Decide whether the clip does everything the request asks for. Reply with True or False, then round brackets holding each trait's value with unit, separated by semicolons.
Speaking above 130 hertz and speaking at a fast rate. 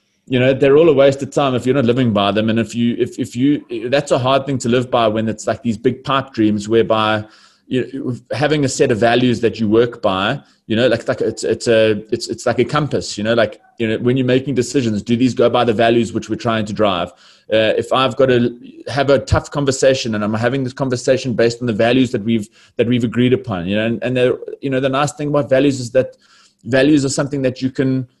False (125 Hz; 255 wpm)